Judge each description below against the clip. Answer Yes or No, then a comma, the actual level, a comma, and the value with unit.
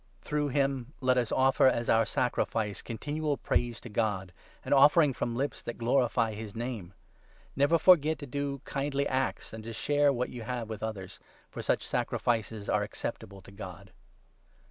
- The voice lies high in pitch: No, low, 125 Hz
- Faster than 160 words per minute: Yes, average, 180 wpm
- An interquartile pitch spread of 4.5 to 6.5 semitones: No, average, 4.1 semitones